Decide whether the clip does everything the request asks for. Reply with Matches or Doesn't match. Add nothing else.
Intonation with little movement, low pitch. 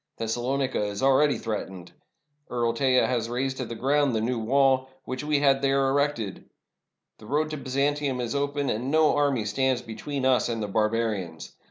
Doesn't match